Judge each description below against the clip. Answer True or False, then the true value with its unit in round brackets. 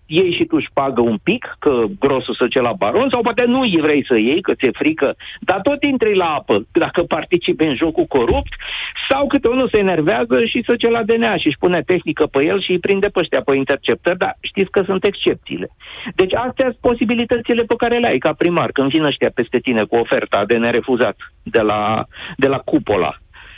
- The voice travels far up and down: True (8.8 semitones)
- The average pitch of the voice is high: True (200 Hz)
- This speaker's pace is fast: True (220 wpm)